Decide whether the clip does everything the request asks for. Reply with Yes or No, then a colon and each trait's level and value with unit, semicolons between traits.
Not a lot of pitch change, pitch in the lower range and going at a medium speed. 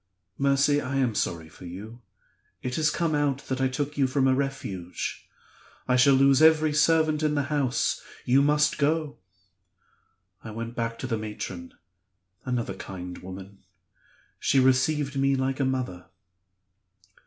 No: average, 4.0 semitones; low, 130 Hz; average, 150 wpm